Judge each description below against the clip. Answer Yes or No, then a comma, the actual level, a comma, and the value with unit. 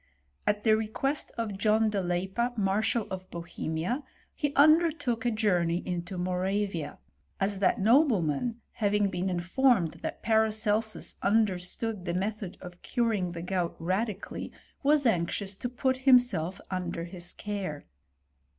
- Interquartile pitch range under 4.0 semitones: No, average, 4.3 semitones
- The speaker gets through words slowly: Yes, slow, 130 wpm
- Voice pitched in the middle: No, high, 205 Hz